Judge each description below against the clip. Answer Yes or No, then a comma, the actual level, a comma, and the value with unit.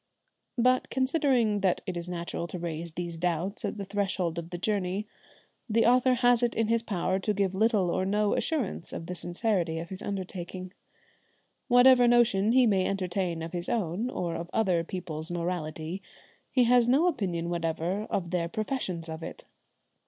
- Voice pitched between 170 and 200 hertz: Yes, high, 190 Hz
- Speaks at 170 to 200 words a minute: Yes, average, 175 wpm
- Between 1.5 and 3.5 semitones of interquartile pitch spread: No, average, 4.8 semitones